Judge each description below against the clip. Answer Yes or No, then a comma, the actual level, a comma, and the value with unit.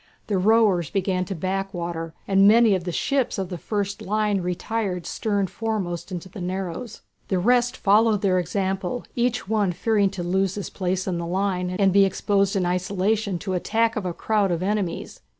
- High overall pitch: Yes, high, 195 Hz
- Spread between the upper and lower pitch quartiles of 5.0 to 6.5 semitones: No, average, 2.7 semitones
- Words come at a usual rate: Yes, average, 185 wpm